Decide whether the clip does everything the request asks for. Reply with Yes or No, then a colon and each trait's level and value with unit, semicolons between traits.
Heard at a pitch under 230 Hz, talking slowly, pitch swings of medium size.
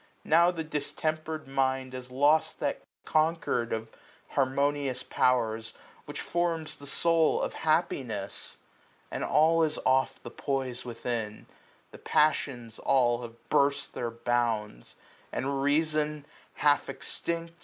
Yes: medium, 140 Hz; slow, 120 wpm; average, 4.3 semitones